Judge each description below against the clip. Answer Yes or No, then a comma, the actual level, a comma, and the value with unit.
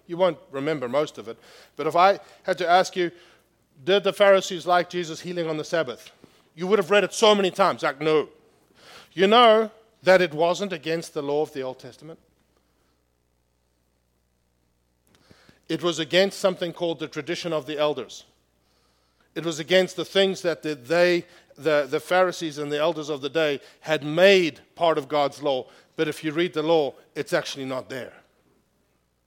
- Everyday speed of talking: Yes, average, 175 wpm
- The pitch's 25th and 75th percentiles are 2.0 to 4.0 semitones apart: No, average, 4.5 semitones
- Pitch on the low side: No, medium, 160 Hz